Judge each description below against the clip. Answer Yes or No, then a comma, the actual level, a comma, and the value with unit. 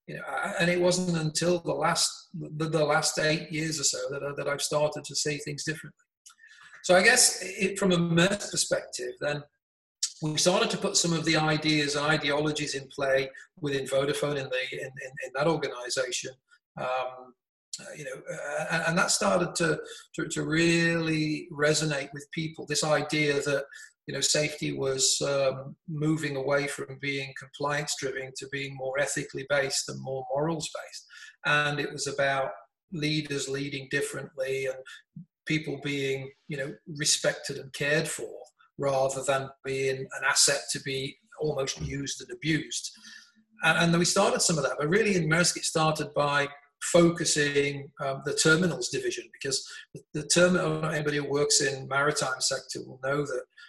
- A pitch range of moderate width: Yes, average, 3.5 semitones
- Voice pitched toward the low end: No, medium, 150 Hz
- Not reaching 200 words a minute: Yes, average, 165 wpm